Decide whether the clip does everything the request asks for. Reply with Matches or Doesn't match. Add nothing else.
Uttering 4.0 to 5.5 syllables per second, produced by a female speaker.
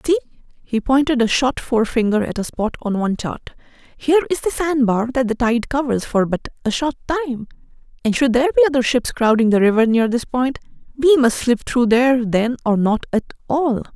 Doesn't match